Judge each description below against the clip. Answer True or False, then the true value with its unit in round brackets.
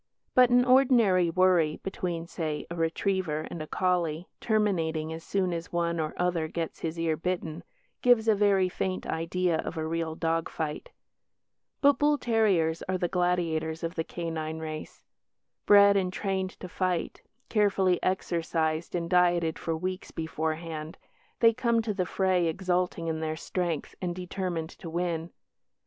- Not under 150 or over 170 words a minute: True (155 wpm)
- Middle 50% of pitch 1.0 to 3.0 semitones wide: True (2.6 semitones)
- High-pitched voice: False (175 Hz)